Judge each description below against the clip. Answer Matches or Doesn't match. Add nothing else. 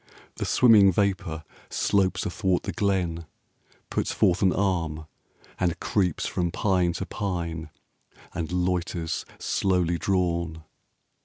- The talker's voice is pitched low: Matches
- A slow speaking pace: Matches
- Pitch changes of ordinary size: Doesn't match